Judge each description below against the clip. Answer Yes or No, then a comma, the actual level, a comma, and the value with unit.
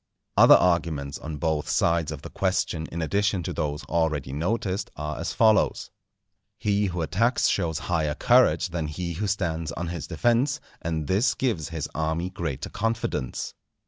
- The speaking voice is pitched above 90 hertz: No, very low, 85 Hz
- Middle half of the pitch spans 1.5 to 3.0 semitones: No, average, 4.2 semitones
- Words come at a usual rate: Yes, average, 160 wpm